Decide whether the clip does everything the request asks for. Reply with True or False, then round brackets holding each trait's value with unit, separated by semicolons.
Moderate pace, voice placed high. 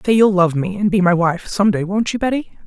False (245 wpm; 205 Hz)